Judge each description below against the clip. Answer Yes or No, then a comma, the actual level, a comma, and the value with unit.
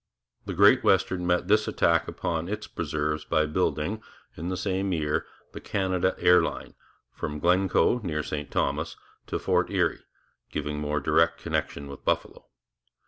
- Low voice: Yes, very low, 85 Hz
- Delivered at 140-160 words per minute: Yes, average, 150 wpm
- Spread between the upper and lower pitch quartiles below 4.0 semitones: Yes, average, 3.4 semitones